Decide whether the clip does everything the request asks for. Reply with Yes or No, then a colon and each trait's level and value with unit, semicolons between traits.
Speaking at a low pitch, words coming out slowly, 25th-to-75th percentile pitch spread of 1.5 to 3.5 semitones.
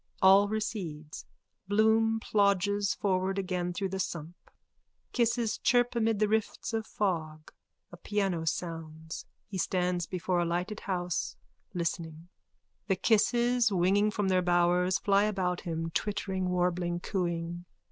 No: medium, 185 Hz; slow, 125 wpm; average, 3.1 semitones